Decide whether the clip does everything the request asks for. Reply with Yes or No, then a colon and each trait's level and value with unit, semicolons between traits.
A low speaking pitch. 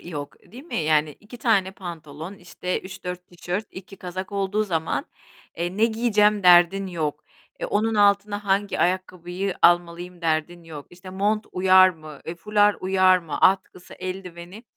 No: medium, 185 Hz